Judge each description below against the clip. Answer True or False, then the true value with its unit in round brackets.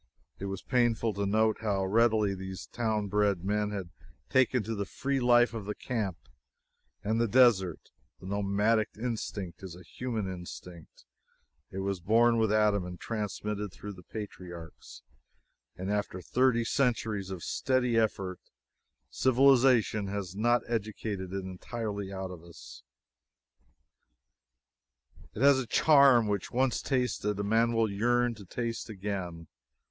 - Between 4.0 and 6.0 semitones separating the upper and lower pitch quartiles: False (3.4 semitones)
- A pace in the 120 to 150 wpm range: True (140 wpm)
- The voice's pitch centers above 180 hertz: False (105 Hz)